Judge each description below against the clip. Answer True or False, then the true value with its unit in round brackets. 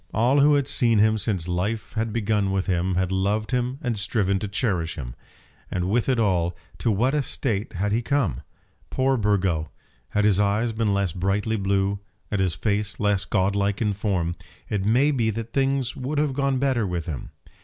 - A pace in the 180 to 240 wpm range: True (195 wpm)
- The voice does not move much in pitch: False (3.7 semitones)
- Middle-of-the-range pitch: False (105 Hz)